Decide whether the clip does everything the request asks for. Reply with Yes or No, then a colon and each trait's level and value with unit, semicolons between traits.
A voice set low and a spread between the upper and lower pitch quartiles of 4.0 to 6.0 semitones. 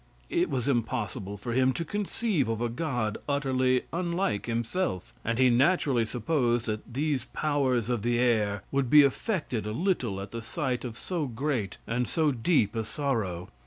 Yes: low, 125 Hz; average, 4.3 semitones